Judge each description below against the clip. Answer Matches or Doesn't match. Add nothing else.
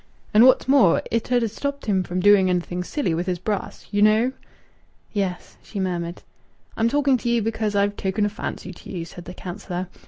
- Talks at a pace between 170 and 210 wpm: Matches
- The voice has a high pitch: Matches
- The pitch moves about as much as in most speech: Matches